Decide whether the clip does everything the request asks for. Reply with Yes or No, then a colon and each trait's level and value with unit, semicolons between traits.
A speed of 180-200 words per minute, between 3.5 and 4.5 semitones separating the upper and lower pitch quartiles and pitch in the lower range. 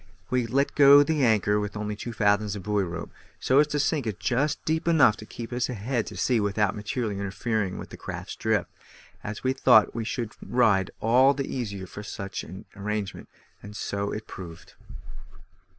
Yes: average, 190 wpm; average, 3.9 semitones; low, 110 Hz